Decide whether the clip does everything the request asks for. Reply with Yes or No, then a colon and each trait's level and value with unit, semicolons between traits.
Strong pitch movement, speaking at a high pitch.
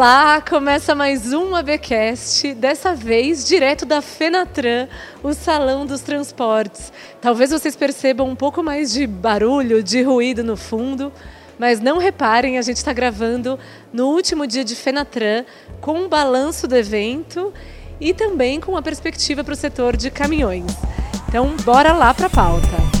No: average, 3.7 semitones; very high, 275 Hz